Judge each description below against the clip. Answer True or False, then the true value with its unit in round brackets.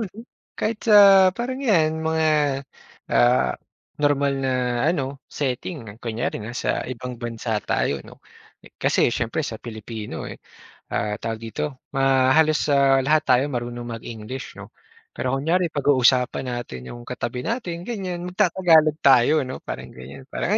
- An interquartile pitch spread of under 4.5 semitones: False (5.1 semitones)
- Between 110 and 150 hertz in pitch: True (135 Hz)